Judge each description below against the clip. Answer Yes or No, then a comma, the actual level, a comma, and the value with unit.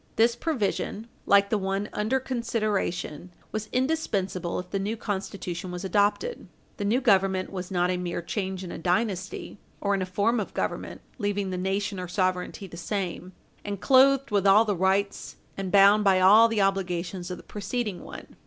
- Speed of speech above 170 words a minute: Yes, average, 180 wpm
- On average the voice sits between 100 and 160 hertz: No, high, 195 Hz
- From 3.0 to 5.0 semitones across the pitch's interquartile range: No, narrow, 2.6 semitones